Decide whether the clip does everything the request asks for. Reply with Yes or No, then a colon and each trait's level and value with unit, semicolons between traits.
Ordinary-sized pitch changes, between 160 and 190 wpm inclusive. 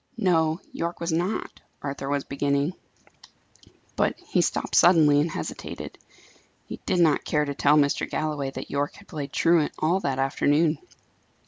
No: average, 3.0 semitones; average, 150 wpm